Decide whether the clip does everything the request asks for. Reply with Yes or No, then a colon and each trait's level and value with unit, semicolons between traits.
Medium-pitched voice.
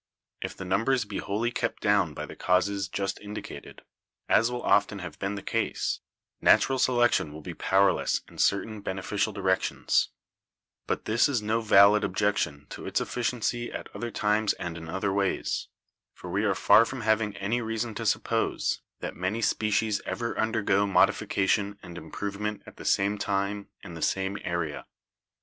No: low, 100 Hz